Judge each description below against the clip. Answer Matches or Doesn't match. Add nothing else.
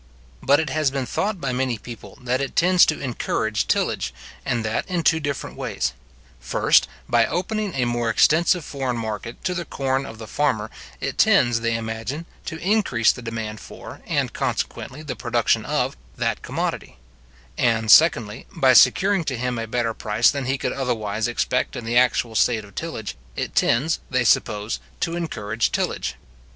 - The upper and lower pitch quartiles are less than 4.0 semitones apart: Doesn't match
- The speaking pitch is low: Matches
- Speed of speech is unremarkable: Matches